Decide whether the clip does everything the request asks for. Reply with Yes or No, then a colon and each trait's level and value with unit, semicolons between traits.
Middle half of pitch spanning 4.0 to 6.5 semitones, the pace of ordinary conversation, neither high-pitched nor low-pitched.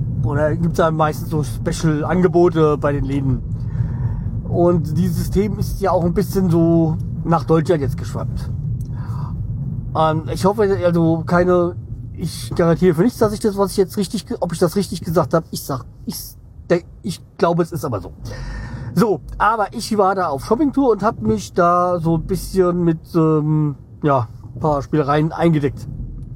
Yes: wide, 5.4 semitones; average, 175 wpm; medium, 160 Hz